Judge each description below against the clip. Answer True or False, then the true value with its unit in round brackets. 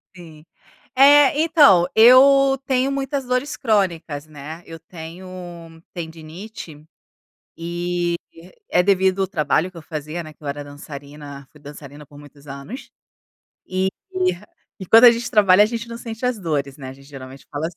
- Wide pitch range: True (7.2 semitones)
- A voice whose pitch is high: False (175 Hz)